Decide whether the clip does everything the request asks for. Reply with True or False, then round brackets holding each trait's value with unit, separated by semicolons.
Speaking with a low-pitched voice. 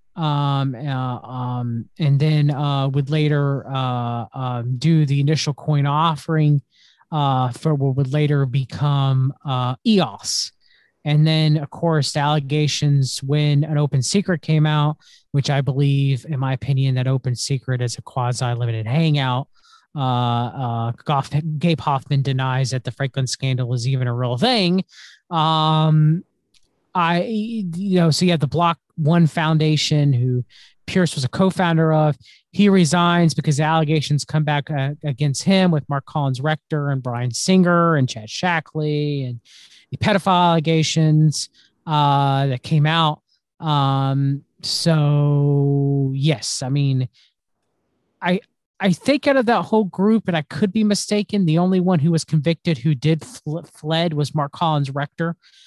False (150 Hz)